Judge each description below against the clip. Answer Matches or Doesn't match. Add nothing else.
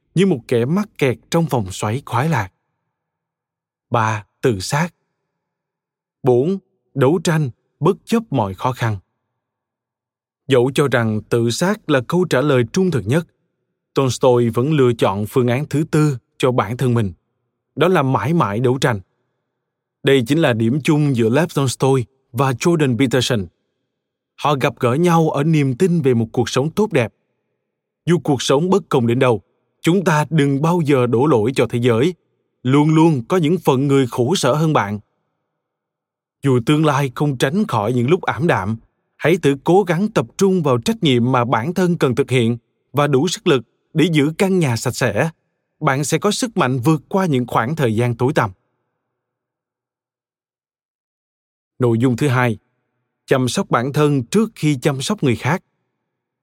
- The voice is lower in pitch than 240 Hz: Matches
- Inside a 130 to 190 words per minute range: Matches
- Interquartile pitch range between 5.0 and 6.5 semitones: Doesn't match